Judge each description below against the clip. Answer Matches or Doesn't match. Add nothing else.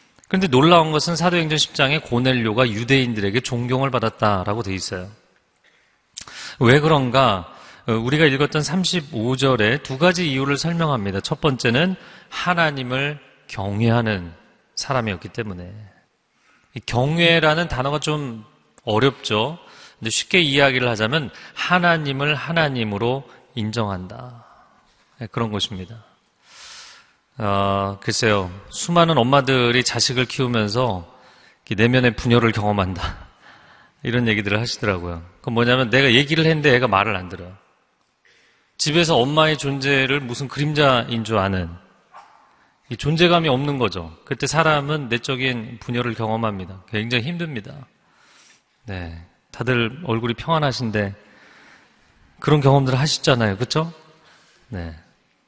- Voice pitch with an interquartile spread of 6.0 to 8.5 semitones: Doesn't match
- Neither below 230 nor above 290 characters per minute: Matches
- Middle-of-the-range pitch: Doesn't match